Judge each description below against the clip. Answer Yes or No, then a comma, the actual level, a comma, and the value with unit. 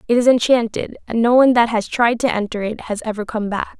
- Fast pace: Yes, fast, 255 wpm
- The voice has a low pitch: No, high, 230 Hz